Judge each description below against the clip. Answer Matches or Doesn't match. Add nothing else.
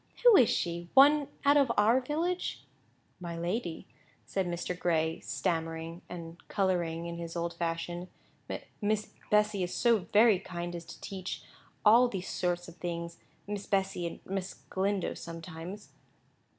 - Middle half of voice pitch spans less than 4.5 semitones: Matches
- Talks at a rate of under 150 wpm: Matches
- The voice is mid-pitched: Matches